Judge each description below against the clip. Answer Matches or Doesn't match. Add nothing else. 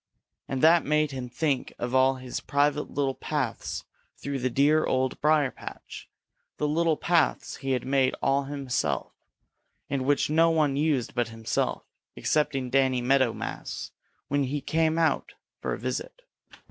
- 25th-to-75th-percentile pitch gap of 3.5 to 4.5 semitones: Doesn't match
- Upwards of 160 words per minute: Doesn't match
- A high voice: Doesn't match